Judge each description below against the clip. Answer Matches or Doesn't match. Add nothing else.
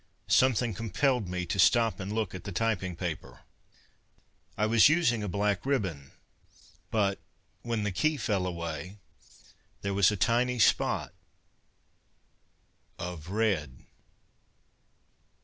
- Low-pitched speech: Matches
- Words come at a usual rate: Doesn't match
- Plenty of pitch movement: Doesn't match